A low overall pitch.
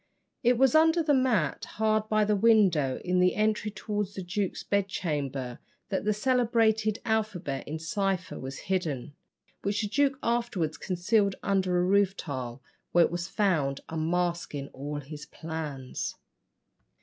No: high, 190 Hz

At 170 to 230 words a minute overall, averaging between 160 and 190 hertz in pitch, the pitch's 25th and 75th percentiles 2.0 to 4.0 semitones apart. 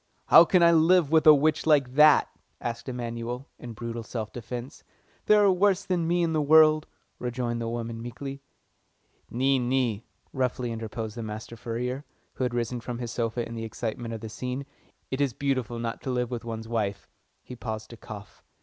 No: average, 195 wpm; low, 125 Hz; average, 3.4 semitones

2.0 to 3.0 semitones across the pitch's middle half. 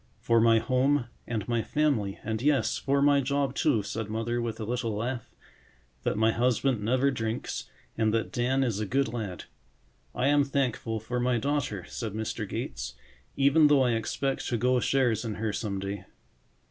No: average, 3.5 semitones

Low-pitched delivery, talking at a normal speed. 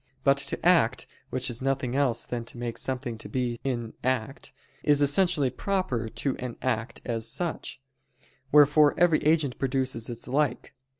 Yes: low, 130 Hz; average, 160 wpm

